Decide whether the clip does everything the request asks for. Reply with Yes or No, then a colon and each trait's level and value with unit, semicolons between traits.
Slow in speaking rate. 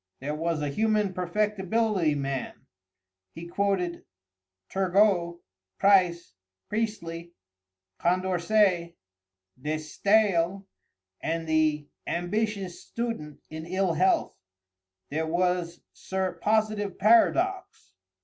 Yes: slow, 85 wpm